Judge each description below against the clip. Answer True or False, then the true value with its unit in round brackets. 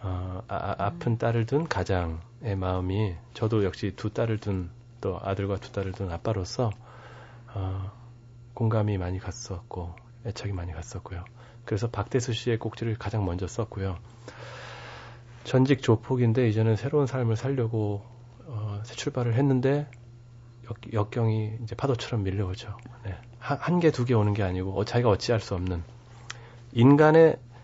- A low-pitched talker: True (115 Hz)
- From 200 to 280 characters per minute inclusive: False (295 characters per minute)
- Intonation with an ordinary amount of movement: True (3.3 semitones)